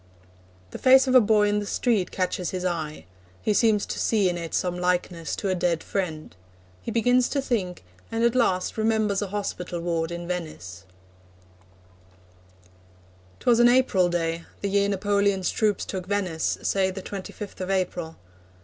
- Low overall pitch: No, high, 190 Hz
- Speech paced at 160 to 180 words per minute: Yes, average, 165 wpm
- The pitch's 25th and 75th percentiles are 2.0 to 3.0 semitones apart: No, average, 3.4 semitones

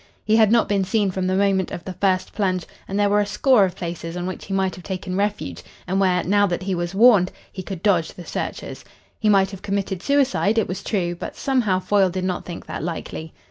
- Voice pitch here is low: No, high, 190 Hz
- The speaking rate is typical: No, fast, 240 wpm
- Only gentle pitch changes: Yes, narrow, 2.1 semitones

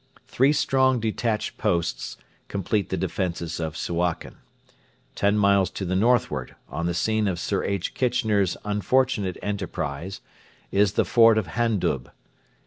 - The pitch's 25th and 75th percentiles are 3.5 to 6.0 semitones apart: Yes, average, 4.3 semitones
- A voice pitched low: Yes, low, 100 Hz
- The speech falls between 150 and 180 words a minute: No, slow, 135 wpm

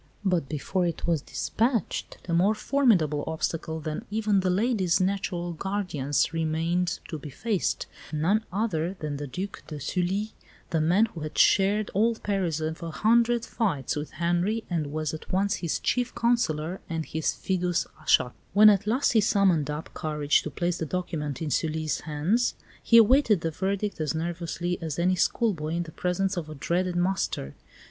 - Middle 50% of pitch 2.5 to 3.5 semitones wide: No, average, 4.3 semitones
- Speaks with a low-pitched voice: No, medium, 175 Hz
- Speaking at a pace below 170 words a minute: No, average, 175 wpm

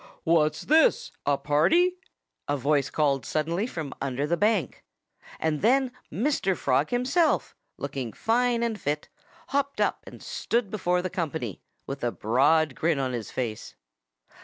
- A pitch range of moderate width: No, wide, 8.7 semitones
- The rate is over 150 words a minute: No, average, 145 wpm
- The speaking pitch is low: No, medium, 160 Hz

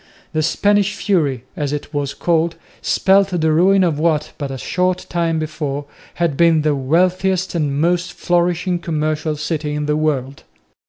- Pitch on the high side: No, medium, 160 Hz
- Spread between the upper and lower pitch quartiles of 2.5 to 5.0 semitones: Yes, average, 3.1 semitones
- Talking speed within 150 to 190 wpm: Yes, average, 160 wpm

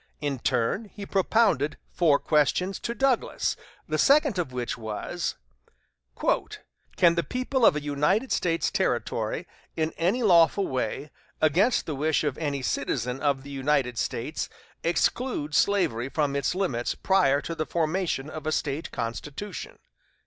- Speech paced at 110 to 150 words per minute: Yes, average, 140 wpm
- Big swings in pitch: Yes, wide, 5.7 semitones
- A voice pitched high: No, medium, 155 Hz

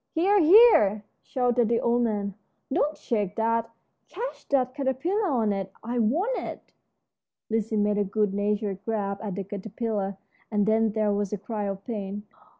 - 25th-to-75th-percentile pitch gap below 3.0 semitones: No, average, 3.4 semitones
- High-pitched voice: Yes, high, 220 Hz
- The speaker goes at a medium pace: Yes, average, 160 wpm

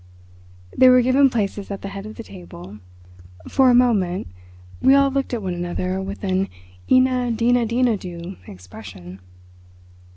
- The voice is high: Yes, high, 205 Hz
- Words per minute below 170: Yes, average, 155 wpm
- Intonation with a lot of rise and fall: Yes, wide, 6.0 semitones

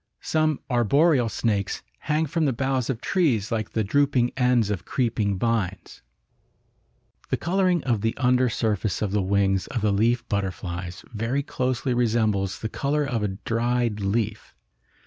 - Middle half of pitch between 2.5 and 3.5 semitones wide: No, average, 4.2 semitones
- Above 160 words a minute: No, average, 150 wpm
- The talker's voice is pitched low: Yes, low, 115 Hz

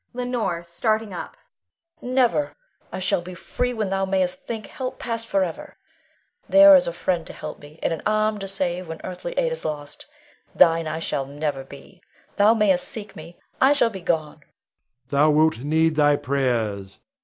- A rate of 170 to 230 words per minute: Yes, average, 180 wpm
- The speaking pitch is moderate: Yes, medium, 180 Hz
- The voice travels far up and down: Yes, wide, 6.2 semitones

